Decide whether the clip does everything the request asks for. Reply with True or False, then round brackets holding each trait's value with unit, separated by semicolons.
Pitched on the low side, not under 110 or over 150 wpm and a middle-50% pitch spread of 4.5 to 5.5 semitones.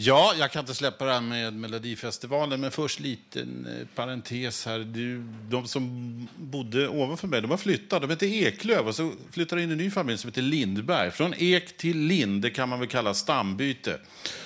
False (130 Hz; 195 wpm; 5.2 semitones)